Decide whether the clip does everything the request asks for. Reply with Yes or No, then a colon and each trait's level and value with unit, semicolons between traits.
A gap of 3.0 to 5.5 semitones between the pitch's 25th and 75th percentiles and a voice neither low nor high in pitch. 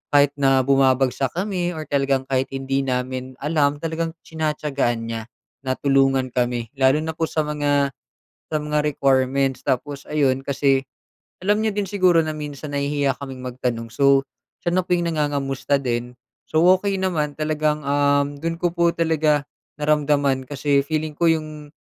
No: narrow, 2.6 semitones; medium, 145 Hz